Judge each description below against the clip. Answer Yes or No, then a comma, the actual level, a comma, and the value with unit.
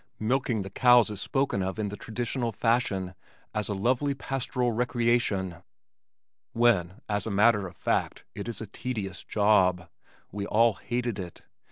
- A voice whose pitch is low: Yes, low, 110 Hz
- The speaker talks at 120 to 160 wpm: Yes, average, 155 wpm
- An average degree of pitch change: Yes, average, 3.6 semitones